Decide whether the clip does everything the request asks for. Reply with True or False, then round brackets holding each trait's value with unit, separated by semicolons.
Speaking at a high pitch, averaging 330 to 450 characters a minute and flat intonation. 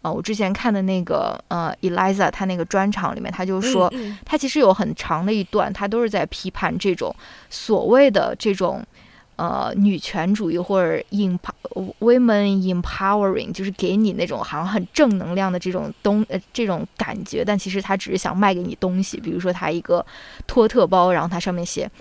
True (195 Hz; 335 characters per minute; 2.1 semitones)